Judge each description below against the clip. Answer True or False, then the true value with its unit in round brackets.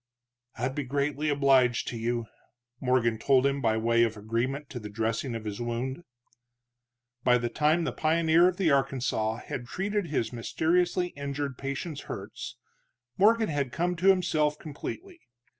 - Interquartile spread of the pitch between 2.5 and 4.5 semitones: False (5.2 semitones)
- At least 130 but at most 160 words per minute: True (155 wpm)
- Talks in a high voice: False (140 Hz)